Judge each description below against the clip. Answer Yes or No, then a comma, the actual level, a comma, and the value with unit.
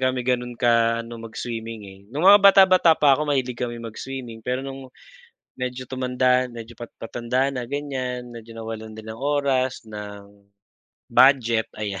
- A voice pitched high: No, low, 125 Hz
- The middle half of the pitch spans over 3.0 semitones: No, narrow, 2.5 semitones